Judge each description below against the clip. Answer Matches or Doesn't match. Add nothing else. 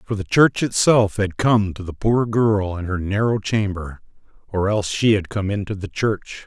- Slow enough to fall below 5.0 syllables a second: Matches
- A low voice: Matches